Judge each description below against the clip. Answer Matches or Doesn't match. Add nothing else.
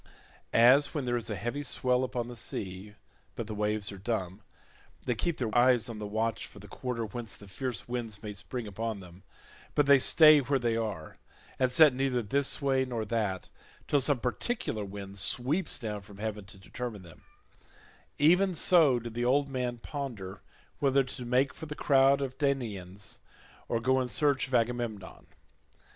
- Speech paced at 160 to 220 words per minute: Matches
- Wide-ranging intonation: Doesn't match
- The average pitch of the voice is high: Doesn't match